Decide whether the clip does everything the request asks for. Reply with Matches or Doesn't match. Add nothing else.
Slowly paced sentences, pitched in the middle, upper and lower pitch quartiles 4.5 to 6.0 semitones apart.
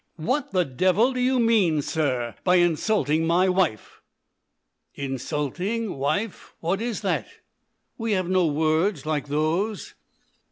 Matches